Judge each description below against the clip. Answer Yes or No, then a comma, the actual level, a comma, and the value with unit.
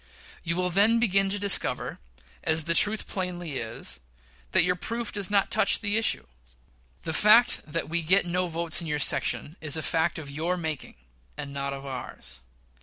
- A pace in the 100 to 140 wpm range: No, average, 180 wpm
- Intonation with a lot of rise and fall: No, average, 4.2 semitones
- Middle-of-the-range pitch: Yes, medium, 170 Hz